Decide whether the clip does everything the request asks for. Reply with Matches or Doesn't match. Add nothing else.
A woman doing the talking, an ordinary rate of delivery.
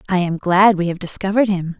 Doesn't match